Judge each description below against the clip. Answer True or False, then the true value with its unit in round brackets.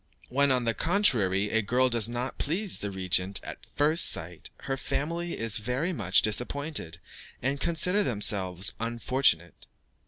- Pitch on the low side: True (120 Hz)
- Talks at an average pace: True (145 wpm)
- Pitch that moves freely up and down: True (6.4 semitones)